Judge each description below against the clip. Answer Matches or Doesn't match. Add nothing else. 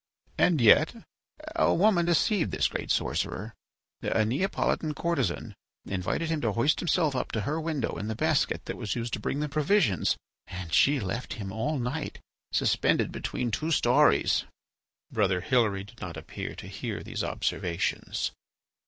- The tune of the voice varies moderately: Doesn't match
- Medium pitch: Doesn't match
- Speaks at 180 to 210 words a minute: Doesn't match